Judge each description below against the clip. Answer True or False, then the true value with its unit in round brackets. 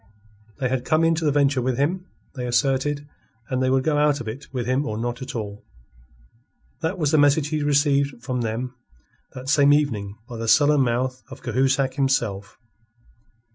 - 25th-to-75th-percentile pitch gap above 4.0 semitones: False (2.9 semitones)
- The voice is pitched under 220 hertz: True (135 Hz)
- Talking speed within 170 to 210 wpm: True (180 wpm)